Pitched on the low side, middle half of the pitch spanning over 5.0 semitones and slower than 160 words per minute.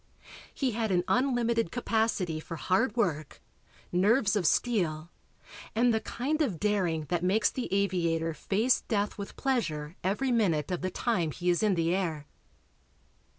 No: high, 195 Hz; wide, 5.4 semitones; average, 150 wpm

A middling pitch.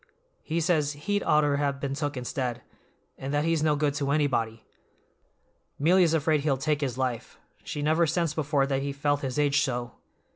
Yes: medium, 145 Hz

